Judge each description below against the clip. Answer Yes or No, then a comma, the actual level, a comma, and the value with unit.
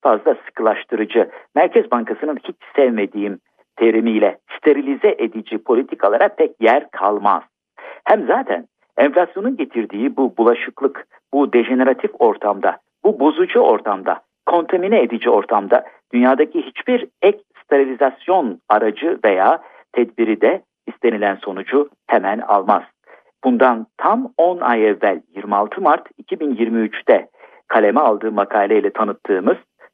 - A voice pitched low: Yes, low, 130 Hz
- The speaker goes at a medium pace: Yes, average, 105 wpm